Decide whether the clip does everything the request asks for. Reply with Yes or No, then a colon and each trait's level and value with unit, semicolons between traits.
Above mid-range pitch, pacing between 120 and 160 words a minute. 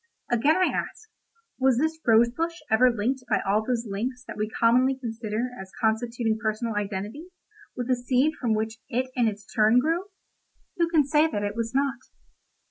No: high, 240 Hz; average, 180 wpm